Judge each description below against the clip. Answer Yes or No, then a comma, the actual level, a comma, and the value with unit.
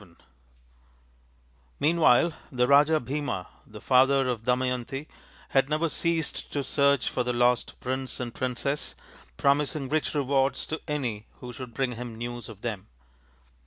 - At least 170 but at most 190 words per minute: No, average, 145 wpm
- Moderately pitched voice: No, low, 130 Hz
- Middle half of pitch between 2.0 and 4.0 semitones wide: Yes, average, 2.9 semitones